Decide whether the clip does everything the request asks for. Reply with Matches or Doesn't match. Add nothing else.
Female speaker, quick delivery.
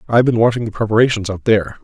Doesn't match